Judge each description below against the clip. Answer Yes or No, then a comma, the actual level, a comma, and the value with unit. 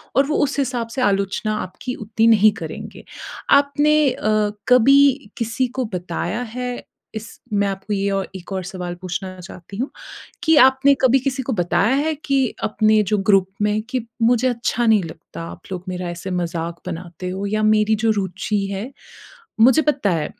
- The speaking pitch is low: No, high, 215 Hz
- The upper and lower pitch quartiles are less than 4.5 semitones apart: No, average, 5.2 semitones